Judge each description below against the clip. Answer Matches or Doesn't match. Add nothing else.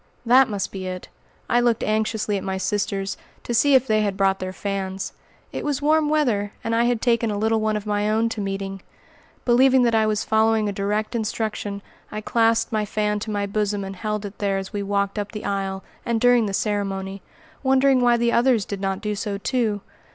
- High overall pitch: Matches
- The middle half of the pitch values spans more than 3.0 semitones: Doesn't match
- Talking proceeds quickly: Matches